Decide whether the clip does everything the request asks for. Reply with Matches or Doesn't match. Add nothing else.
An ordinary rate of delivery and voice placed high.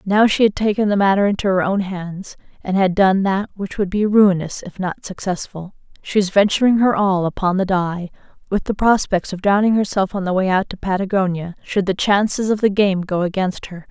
Doesn't match